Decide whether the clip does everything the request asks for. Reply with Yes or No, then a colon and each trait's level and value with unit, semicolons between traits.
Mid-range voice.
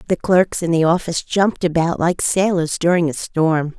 Yes: medium, 170 Hz